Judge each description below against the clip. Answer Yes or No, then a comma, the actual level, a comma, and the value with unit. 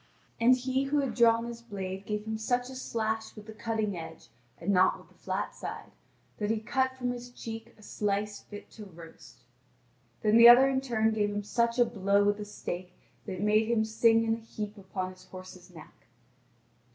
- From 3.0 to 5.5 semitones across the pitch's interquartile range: No, narrow, 2.5 semitones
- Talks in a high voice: Yes, high, 220 Hz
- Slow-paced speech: No, fast, 205 wpm